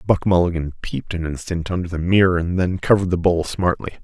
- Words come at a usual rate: No, fast, 210 wpm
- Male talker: Yes, male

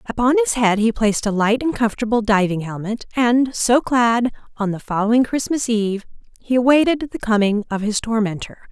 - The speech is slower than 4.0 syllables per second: No, 5.5 syllables/s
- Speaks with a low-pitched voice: No, high, 230 Hz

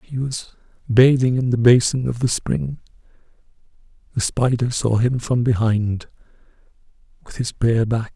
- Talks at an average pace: No, slow, 130 wpm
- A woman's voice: No, male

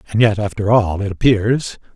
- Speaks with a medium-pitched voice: No, low, 105 Hz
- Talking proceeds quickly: No, average, 185 wpm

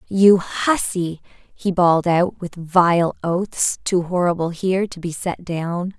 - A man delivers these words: No, female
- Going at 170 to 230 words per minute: No, average, 150 wpm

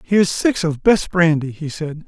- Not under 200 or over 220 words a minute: Yes, fast, 205 wpm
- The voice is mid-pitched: Yes, medium, 165 Hz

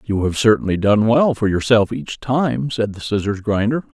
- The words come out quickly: No, average, 195 wpm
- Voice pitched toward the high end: No, low, 110 Hz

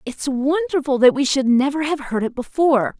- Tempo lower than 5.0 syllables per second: No, 5.2 syllables/s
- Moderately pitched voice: No, very high, 275 Hz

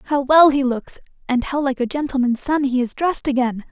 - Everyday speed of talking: No, fast, 225 wpm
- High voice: Yes, very high, 265 Hz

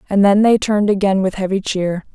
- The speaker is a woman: Yes, female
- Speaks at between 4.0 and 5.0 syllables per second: No, 5.8 syllables/s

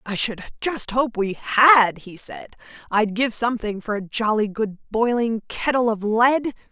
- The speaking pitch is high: Yes, high, 225 Hz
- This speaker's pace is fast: No, average, 170 wpm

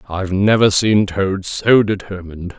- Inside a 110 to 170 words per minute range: Yes, average, 140 wpm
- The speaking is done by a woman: No, male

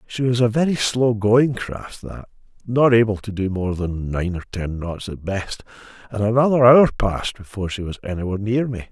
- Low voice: Yes, low, 110 Hz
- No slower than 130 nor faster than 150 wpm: No, average, 190 wpm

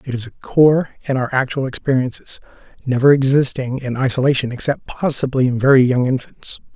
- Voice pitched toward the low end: Yes, low, 130 Hz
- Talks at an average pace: Yes, average, 160 wpm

